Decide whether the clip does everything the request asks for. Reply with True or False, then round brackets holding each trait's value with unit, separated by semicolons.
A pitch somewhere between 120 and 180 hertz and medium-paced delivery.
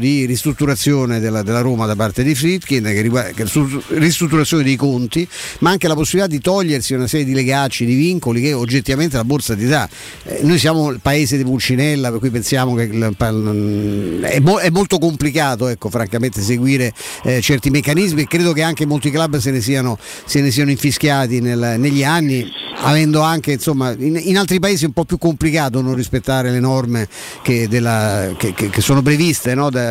False (135 Hz; 195 wpm)